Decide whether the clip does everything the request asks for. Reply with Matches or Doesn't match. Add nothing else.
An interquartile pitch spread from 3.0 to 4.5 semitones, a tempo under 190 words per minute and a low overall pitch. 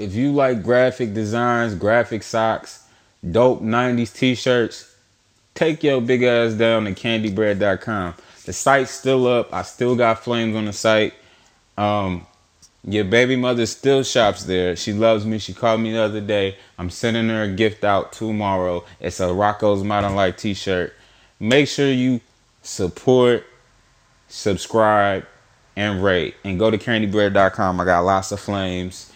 Matches